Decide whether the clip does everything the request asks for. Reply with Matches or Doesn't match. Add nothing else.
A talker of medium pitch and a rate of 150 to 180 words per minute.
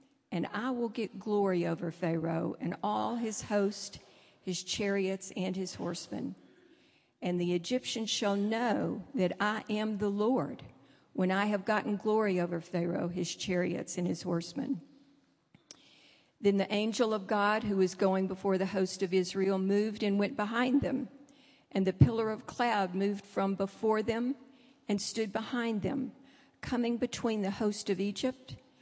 Doesn't match